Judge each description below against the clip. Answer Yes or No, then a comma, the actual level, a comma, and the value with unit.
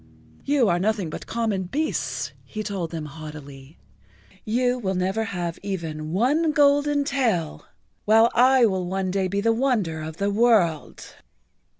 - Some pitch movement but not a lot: No, wide, 6.0 semitones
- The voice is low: No, high, 200 Hz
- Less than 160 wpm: Yes, average, 145 wpm